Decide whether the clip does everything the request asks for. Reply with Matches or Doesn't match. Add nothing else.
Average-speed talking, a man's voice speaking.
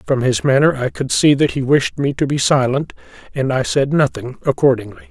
Doesn't match